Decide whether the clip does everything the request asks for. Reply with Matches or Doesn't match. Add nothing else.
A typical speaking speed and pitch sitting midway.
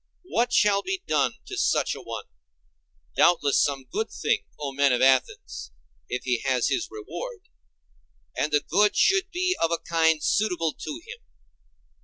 Matches